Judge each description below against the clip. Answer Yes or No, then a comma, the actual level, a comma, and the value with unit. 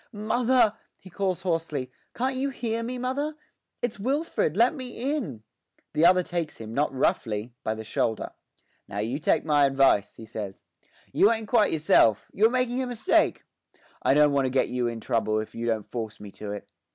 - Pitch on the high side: No, medium, 160 Hz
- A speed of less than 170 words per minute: No, average, 190 wpm